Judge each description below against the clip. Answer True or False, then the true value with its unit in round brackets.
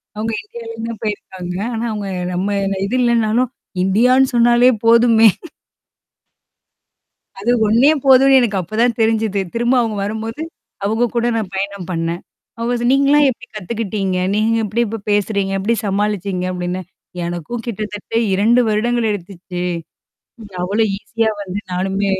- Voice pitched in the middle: False (215 Hz)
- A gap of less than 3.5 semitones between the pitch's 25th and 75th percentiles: True (3.1 semitones)